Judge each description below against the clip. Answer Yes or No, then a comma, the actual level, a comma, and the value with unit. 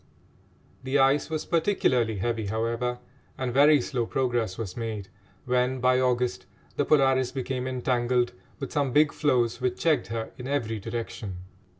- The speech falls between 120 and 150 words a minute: Yes, average, 145 wpm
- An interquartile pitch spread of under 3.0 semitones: Yes, narrow, 2.6 semitones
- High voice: No, low, 125 Hz